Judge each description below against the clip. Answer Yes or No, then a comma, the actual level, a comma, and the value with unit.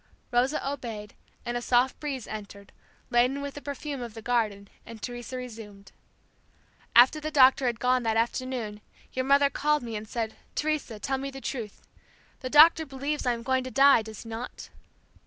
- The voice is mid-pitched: No, very high, 250 Hz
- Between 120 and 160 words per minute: No, average, 180 wpm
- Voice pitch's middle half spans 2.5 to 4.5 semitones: Yes, average, 3.4 semitones